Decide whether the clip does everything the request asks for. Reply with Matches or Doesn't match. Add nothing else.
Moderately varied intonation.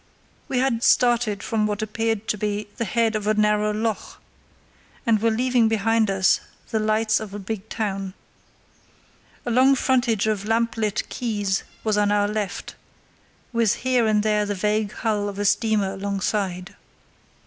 Doesn't match